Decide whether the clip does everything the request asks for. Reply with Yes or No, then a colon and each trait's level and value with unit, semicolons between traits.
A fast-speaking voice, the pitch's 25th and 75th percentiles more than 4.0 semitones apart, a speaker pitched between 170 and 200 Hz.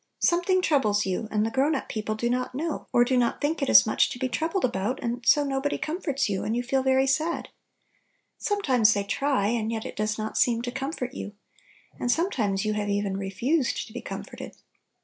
No: fast, 210 wpm; average, 4.6 semitones; high, 245 Hz